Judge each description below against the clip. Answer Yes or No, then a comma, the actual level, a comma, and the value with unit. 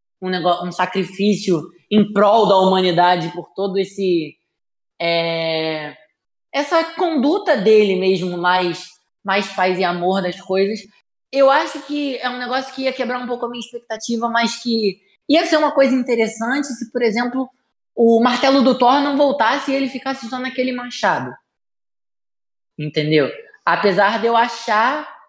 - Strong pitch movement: Yes, wide, 5.9 semitones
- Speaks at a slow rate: No, average, 150 wpm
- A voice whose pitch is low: No, high, 225 Hz